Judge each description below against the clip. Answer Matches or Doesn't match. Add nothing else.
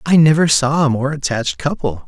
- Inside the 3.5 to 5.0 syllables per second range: Doesn't match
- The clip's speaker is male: Matches